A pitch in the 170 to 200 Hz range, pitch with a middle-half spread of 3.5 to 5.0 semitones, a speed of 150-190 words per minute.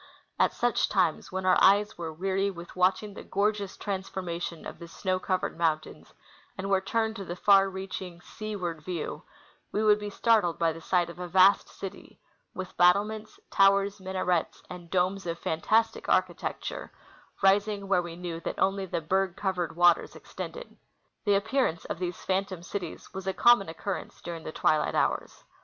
No: high, 190 Hz; narrow, 2.4 semitones; average, 170 wpm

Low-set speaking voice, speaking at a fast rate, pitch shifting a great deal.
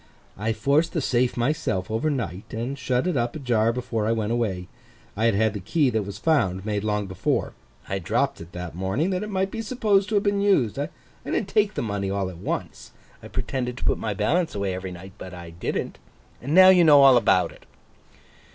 Yes: low, 115 Hz; fast, 215 wpm; wide, 7.8 semitones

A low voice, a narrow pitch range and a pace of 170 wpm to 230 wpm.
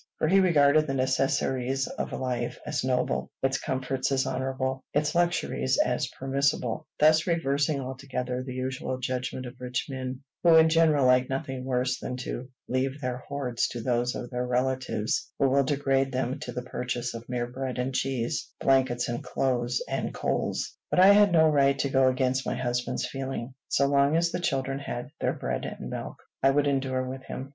Yes: low, 130 Hz; narrow, 1.7 semitones; average, 185 wpm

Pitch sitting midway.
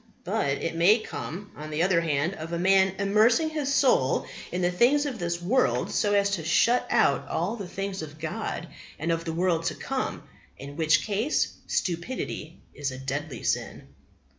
Yes: medium, 175 Hz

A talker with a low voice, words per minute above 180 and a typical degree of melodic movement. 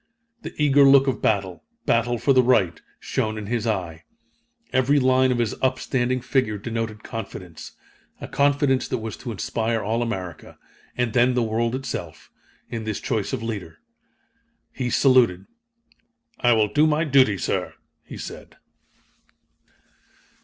No: low, 120 Hz; average, 145 wpm; average, 3.2 semitones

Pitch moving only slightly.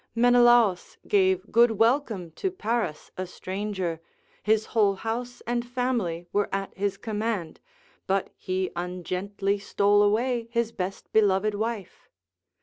No: average, 3.7 semitones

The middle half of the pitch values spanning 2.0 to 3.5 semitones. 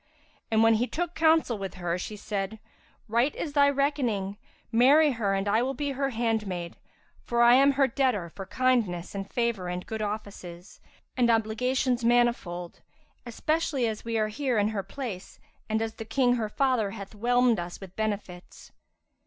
No: average, 4.2 semitones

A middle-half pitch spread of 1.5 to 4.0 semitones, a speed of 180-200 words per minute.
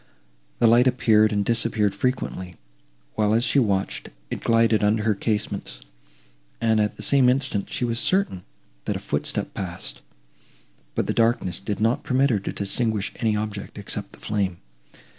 No: narrow, 2.6 semitones; average, 160 wpm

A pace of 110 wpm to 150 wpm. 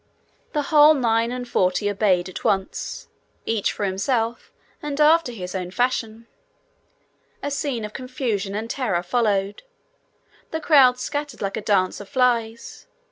Yes: average, 140 wpm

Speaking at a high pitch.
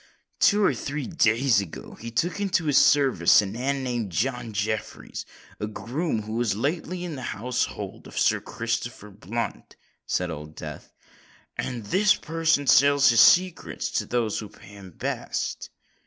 No: low, 120 Hz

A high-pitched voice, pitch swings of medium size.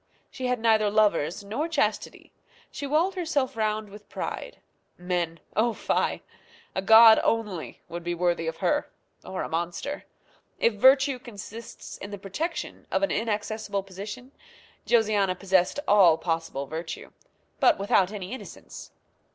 Yes: high, 210 Hz; average, 4.8 semitones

